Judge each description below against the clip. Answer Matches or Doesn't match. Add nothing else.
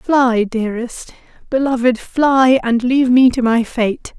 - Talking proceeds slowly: Matches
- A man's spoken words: Doesn't match